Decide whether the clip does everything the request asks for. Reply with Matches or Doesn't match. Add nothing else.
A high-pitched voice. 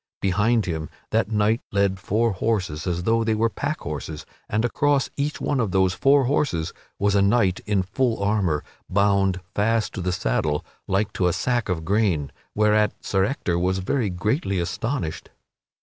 Doesn't match